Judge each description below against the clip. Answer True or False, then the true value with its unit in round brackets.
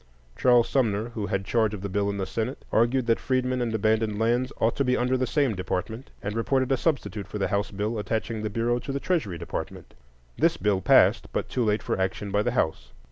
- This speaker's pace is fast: True (230 wpm)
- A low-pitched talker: True (110 Hz)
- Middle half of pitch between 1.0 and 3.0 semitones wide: False (3.5 semitones)